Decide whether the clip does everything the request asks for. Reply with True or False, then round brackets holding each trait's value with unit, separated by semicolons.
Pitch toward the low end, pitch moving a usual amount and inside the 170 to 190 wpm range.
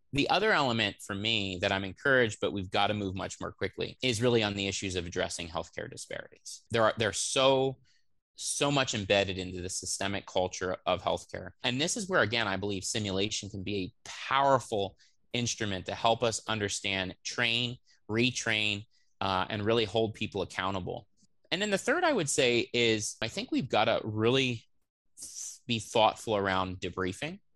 True (105 Hz; 3.8 semitones; 180 wpm)